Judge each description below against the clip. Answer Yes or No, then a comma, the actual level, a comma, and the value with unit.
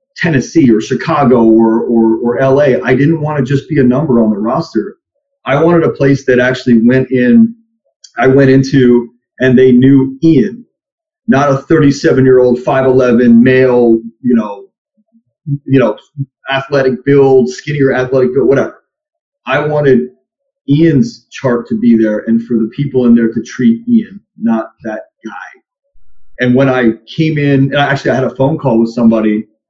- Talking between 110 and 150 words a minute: No, average, 165 wpm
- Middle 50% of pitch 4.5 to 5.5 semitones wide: Yes, average, 4.9 semitones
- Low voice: Yes, low, 130 Hz